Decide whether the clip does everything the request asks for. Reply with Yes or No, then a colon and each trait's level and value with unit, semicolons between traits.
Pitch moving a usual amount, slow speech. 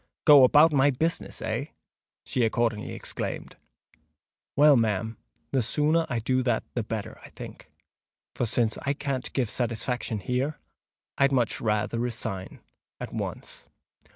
Yes: average, 3.7 semitones; slow, 130 wpm